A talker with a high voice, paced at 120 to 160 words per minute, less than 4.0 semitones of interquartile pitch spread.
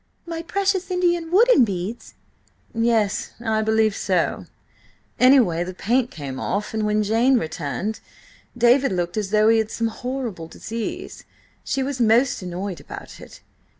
No: high, 220 Hz; average, 140 wpm; average, 4.8 semitones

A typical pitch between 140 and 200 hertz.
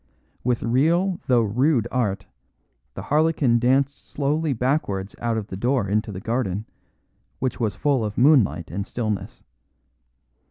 No: low, 120 Hz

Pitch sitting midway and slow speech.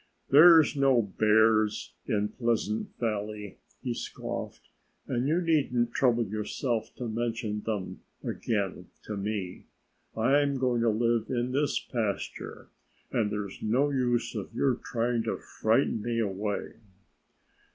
No: low, 115 Hz; slow, 130 wpm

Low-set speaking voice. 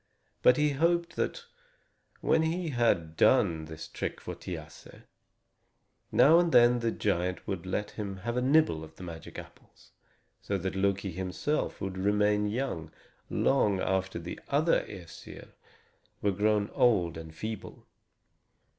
Yes: low, 100 Hz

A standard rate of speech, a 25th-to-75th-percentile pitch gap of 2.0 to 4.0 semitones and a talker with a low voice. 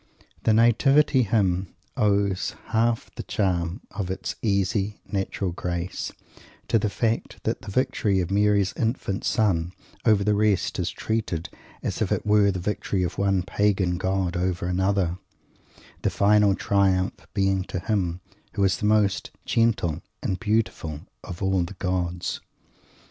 Yes: average, 145 wpm; narrow, 2.4 semitones; low, 100 Hz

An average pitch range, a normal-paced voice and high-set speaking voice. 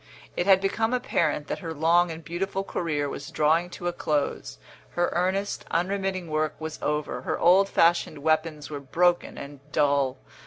No: average, 3.2 semitones; average, 165 wpm; medium, 165 Hz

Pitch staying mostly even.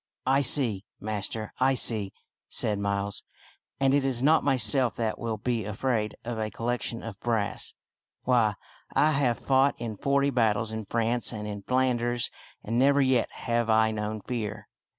No: average, 3.2 semitones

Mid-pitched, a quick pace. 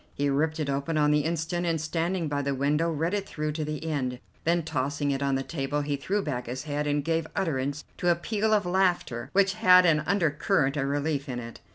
Yes: medium, 150 Hz; fast, 230 wpm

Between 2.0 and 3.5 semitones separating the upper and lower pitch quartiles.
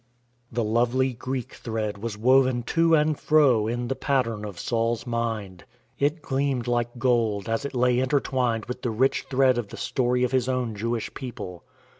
Yes: narrow, 2.6 semitones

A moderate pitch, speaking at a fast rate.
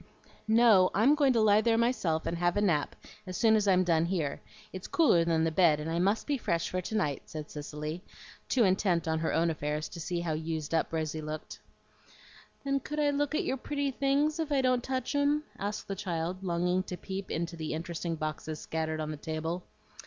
Yes: medium, 180 Hz; fast, 215 wpm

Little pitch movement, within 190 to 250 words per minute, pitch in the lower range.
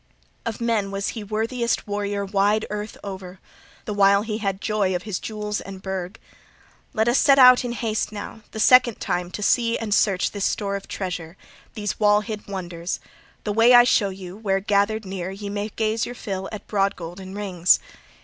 No: narrow, 2.2 semitones; average, 195 wpm; high, 205 Hz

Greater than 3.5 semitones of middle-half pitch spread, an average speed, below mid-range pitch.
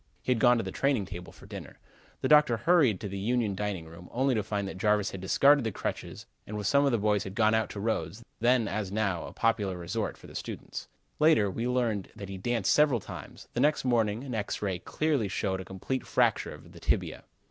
No: average, 4.0 semitones; fast, 235 wpm; low, 110 Hz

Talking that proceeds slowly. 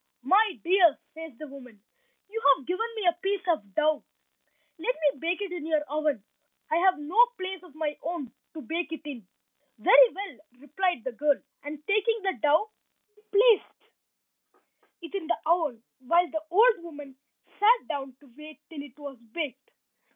No: average, 175 wpm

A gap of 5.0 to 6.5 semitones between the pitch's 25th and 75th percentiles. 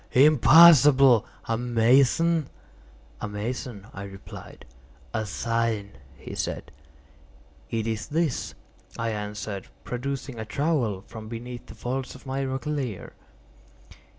No: average, 3.9 semitones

